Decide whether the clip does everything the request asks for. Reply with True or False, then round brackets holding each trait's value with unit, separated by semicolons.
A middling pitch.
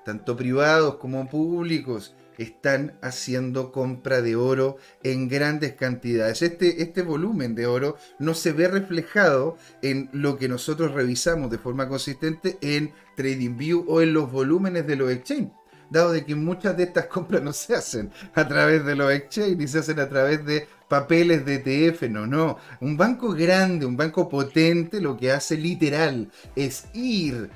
True (145 Hz)